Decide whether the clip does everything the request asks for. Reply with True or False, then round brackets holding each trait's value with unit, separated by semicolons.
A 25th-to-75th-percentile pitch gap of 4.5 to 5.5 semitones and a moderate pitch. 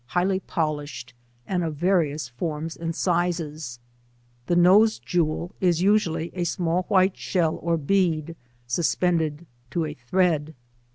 False (2.7 semitones; 170 Hz)